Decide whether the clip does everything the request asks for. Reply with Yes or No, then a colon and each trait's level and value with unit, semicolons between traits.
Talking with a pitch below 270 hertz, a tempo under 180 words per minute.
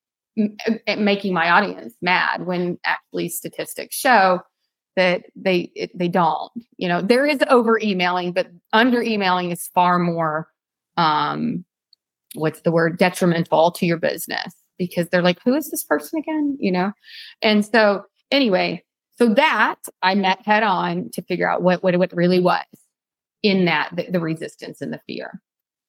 Yes: medium, 185 Hz; average, 160 wpm